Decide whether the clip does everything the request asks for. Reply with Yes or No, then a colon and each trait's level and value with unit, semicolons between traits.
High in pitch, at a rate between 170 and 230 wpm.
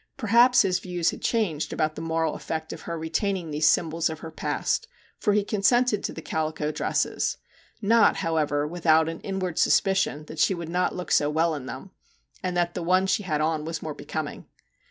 No: medium, 165 Hz; average, 195 wpm